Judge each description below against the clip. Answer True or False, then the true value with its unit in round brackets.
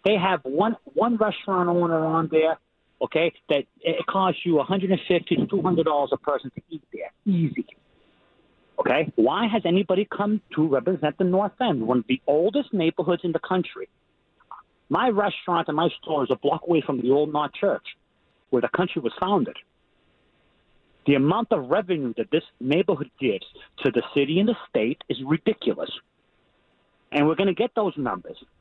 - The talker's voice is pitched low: False (175 Hz)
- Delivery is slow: False (170 wpm)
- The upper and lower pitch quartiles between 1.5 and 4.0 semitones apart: False (4.7 semitones)